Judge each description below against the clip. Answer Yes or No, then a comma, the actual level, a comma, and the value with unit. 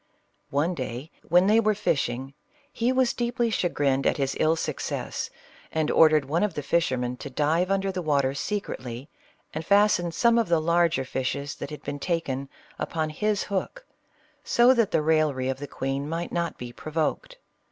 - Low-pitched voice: No, medium, 160 Hz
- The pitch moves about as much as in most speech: No, wide, 6.0 semitones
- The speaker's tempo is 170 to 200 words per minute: Yes, average, 175 wpm